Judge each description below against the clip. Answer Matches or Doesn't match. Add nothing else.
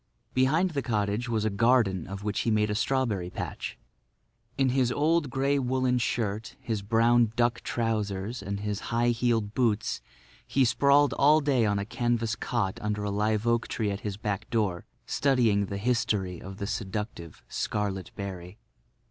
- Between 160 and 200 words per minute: Matches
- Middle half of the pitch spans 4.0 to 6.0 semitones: Doesn't match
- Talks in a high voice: Doesn't match